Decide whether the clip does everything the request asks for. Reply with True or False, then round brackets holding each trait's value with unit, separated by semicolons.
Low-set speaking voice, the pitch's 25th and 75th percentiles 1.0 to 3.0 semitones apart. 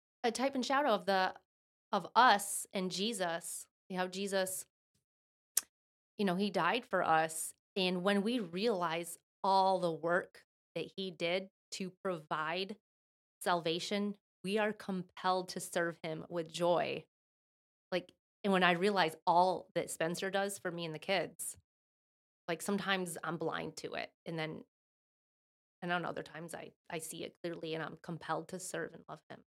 False (185 Hz; 2.5 semitones)